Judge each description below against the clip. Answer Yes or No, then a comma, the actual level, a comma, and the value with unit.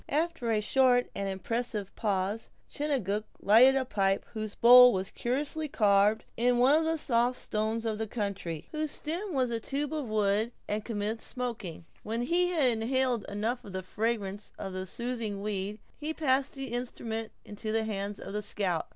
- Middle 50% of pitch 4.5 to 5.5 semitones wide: No, average, 3.9 semitones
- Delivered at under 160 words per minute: No, average, 180 wpm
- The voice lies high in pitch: Yes, high, 225 Hz